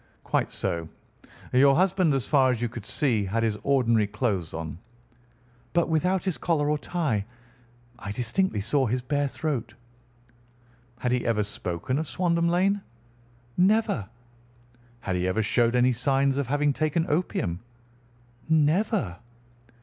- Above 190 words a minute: No, average, 140 wpm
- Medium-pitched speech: No, low, 130 Hz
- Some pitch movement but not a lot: No, wide, 6.3 semitones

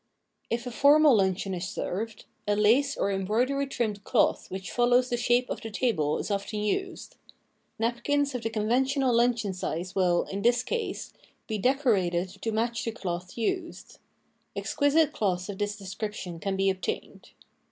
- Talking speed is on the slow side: No, average, 165 wpm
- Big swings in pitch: No, average, 4.4 semitones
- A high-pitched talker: Yes, high, 220 Hz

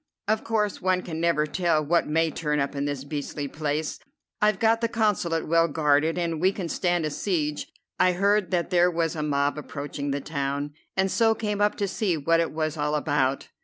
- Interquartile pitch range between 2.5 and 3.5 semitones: No, average, 4.0 semitones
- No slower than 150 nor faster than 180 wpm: No, fast, 205 wpm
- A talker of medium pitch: Yes, medium, 165 Hz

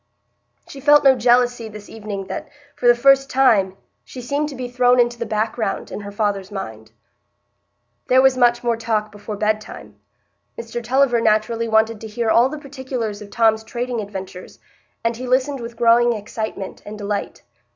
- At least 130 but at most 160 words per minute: No, average, 170 wpm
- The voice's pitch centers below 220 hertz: No, high, 230 Hz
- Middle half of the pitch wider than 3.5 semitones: No, average, 2.9 semitones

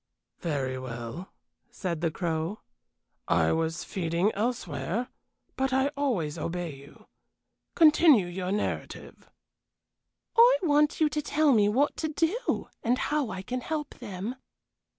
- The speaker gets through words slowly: Yes, slow, 130 wpm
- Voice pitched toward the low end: No, high, 210 Hz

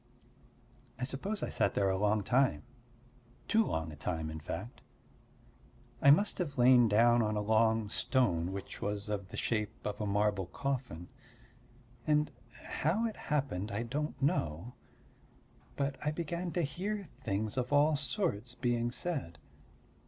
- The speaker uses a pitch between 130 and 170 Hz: No, low, 120 Hz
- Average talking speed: Yes, average, 150 wpm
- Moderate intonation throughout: No, wide, 6.1 semitones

